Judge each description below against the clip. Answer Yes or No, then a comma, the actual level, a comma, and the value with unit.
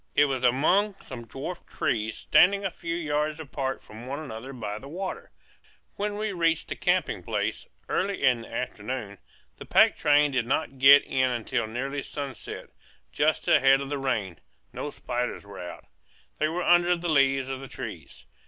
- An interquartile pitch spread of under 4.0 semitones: No, average, 4.4 semitones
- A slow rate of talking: No, average, 175 wpm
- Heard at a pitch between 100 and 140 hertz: Yes, low, 135 Hz